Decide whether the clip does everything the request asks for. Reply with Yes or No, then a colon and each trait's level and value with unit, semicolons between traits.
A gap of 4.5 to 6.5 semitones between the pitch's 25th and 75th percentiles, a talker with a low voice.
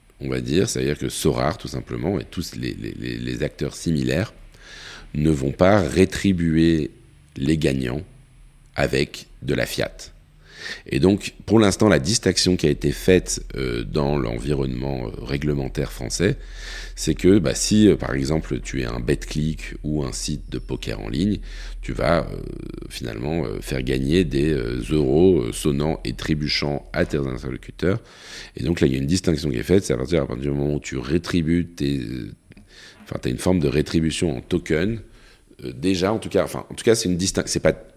Yes: average, 5.3 semitones; very low, 75 Hz